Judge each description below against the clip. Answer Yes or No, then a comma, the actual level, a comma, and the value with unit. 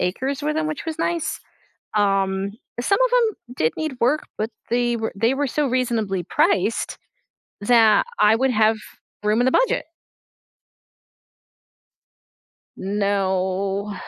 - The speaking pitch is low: No, high, 225 Hz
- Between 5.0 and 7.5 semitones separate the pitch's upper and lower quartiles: Yes, wide, 5.5 semitones